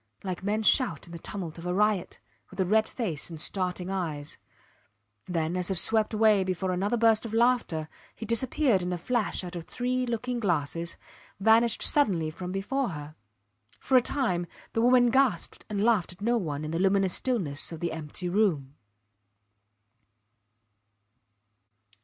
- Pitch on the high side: Yes, high, 195 Hz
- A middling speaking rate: Yes, average, 165 wpm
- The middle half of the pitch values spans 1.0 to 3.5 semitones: No, average, 4.9 semitones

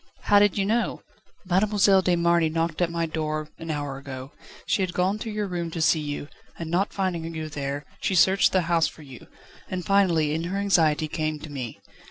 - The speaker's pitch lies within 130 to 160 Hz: No, medium, 170 Hz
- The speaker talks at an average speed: No, fast, 210 wpm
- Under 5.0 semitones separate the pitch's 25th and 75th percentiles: Yes, average, 3.6 semitones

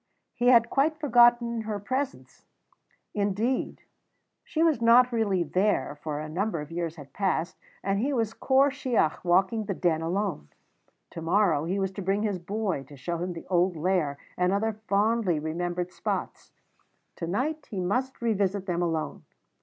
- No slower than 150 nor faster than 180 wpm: Yes, average, 165 wpm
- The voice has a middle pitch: No, high, 195 Hz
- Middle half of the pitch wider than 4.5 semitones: Yes, average, 5.0 semitones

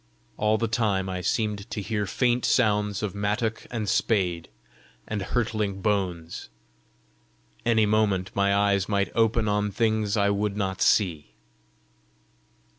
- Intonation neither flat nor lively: No, narrow, 1.8 semitones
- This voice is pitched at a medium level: No, low, 105 Hz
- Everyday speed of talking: No, slow, 130 wpm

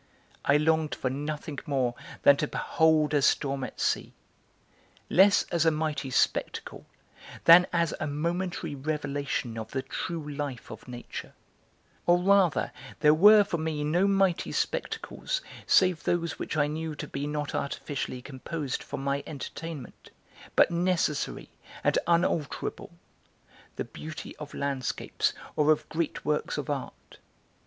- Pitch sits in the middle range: Yes, medium, 150 Hz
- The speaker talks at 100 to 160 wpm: Yes, average, 140 wpm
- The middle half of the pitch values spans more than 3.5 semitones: No, average, 2.9 semitones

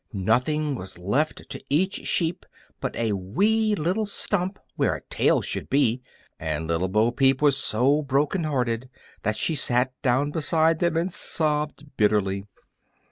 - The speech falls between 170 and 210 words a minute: No, average, 150 wpm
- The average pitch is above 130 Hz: Yes, medium, 140 Hz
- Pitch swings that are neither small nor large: No, wide, 6.9 semitones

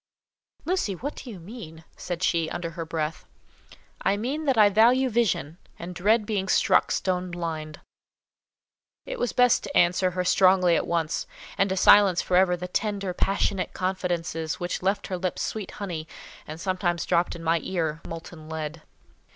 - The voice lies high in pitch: No, medium, 180 Hz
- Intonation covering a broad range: No, average, 3.3 semitones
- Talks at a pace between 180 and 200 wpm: No, average, 165 wpm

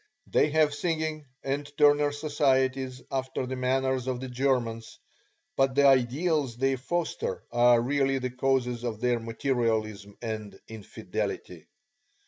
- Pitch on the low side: Yes, low, 130 Hz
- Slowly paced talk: Yes, slow, 125 wpm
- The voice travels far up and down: No, average, 2.8 semitones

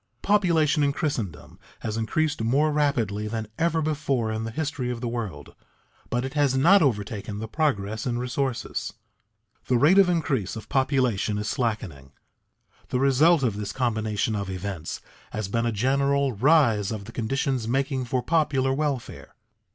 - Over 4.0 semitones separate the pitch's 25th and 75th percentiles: Yes, average, 4.9 semitones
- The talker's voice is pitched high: No, low, 125 Hz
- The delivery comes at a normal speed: Yes, average, 160 wpm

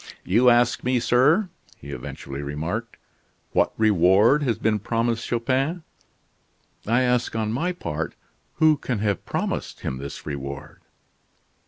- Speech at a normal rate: No, slow, 130 wpm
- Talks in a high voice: No, low, 115 Hz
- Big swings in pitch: Yes, wide, 6.3 semitones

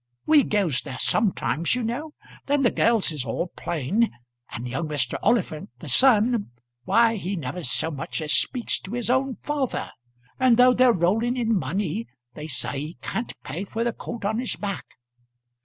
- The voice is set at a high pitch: Yes, high, 205 Hz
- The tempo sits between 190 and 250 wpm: No, average, 175 wpm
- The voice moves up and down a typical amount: No, wide, 7.7 semitones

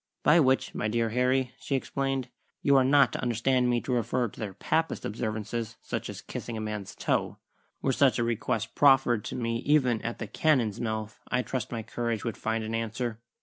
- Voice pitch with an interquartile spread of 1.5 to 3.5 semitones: Yes, average, 2.9 semitones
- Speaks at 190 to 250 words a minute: Yes, average, 200 wpm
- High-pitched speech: No, low, 120 Hz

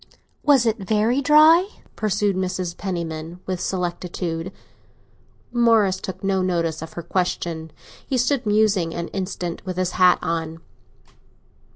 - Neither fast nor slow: No, slow, 130 wpm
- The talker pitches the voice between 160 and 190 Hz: Yes, medium, 185 Hz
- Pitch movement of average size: Yes, average, 4.0 semitones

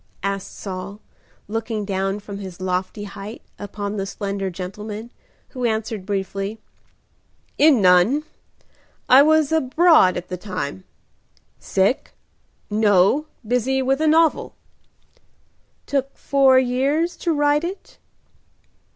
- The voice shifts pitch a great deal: Yes, wide, 5.8 semitones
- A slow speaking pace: Yes, slow, 110 wpm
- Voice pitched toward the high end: Yes, high, 215 Hz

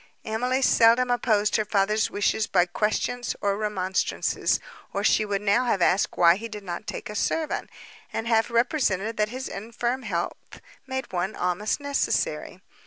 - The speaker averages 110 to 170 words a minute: Yes, average, 160 wpm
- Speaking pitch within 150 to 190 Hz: No, high, 215 Hz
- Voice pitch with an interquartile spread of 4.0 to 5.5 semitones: No, average, 3.3 semitones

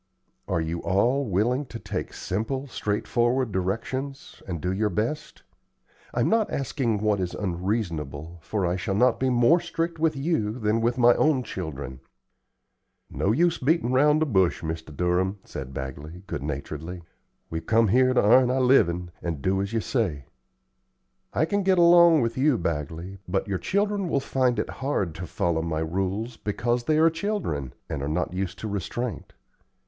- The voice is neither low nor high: No, low, 105 Hz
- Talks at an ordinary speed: Yes, average, 175 wpm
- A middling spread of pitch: No, wide, 7.1 semitones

